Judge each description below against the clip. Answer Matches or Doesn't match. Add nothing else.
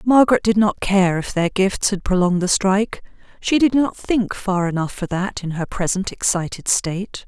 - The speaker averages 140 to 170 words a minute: Doesn't match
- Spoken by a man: Doesn't match